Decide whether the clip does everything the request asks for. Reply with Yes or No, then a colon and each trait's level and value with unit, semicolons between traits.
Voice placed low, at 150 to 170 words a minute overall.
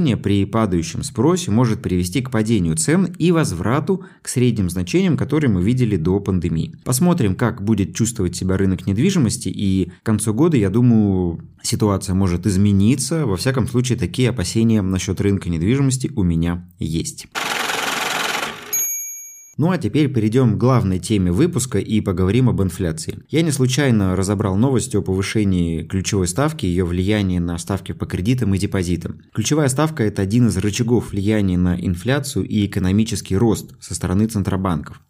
Yes: low, 105 Hz; average, 155 wpm